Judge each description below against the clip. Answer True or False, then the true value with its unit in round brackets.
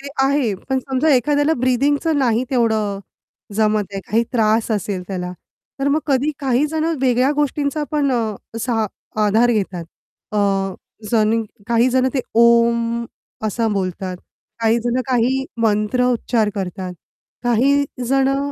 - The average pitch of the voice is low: False (240 Hz)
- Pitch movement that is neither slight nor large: True (3.9 semitones)